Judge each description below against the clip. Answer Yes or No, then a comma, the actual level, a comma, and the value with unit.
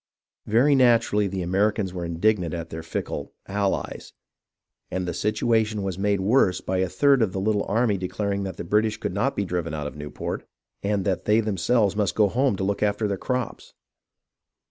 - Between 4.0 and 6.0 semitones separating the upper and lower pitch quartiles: No, average, 2.8 semitones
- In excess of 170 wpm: Yes, average, 190 wpm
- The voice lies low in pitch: Yes, low, 100 Hz